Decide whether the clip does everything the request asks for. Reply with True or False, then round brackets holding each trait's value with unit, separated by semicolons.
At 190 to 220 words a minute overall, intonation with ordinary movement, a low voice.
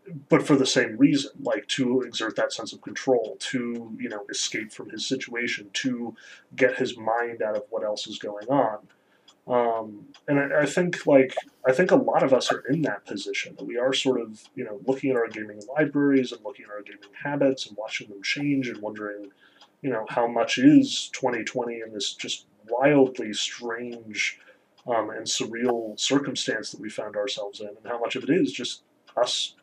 True (200 wpm; 4.0 semitones; 125 Hz)